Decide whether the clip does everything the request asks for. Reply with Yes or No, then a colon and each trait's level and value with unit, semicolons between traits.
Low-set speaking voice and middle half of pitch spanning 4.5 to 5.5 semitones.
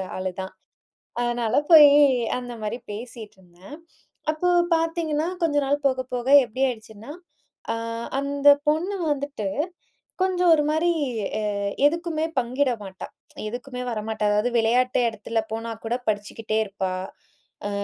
No: high, 245 Hz; average, 5.2 semitones